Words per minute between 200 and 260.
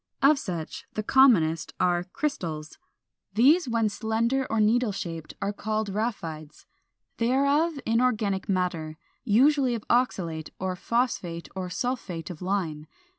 No: slow, 135 wpm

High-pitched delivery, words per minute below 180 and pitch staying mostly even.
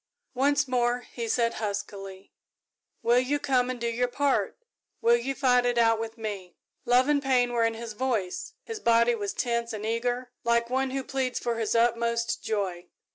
No: high, 235 Hz; average, 185 wpm; narrow, 1.9 semitones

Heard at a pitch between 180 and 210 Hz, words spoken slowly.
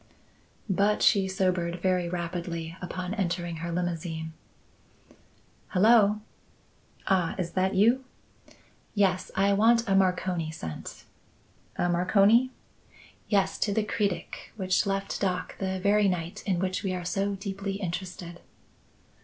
Yes: medium, 185 Hz; slow, 120 wpm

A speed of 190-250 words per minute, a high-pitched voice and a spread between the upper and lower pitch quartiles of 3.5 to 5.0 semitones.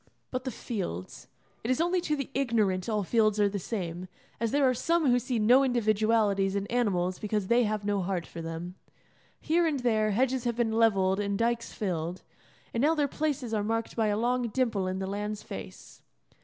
Yes: average, 200 wpm; high, 220 Hz; average, 3.9 semitones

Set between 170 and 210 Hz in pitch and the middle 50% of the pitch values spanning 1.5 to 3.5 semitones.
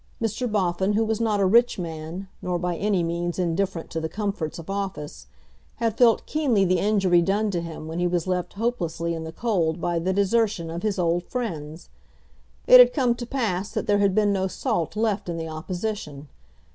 No: high, 190 Hz; average, 4.2 semitones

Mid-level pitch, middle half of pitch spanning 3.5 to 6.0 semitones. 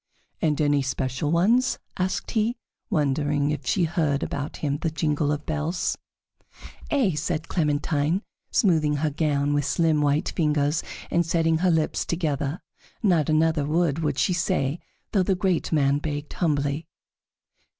No: medium, 155 Hz; average, 2.8 semitones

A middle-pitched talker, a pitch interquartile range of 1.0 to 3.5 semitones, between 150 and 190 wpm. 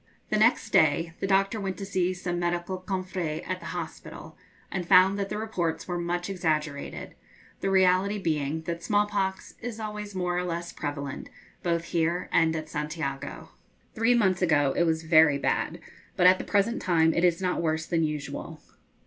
Yes: medium, 175 Hz; average, 3.0 semitones; average, 180 wpm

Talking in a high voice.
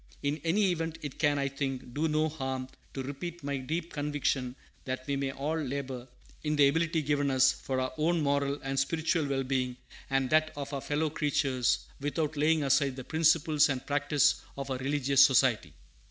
No: medium, 140 Hz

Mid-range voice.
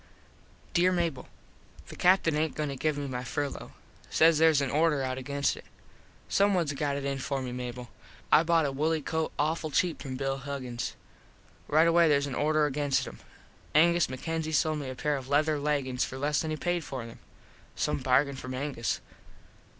Yes: medium, 145 Hz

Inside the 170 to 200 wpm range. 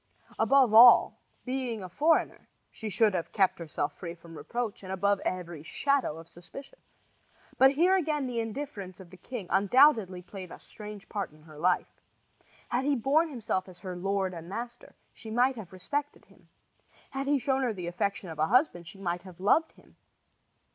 Yes: average, 180 wpm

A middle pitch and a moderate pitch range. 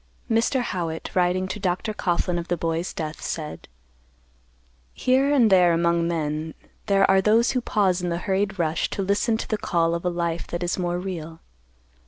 Yes: medium, 180 Hz; average, 3.0 semitones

